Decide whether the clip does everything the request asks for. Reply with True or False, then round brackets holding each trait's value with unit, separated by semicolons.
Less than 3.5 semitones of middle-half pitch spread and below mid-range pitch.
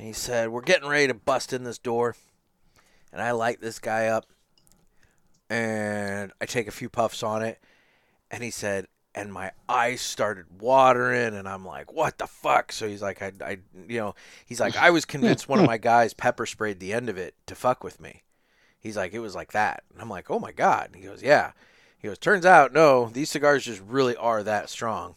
True (2.9 semitones; 115 Hz)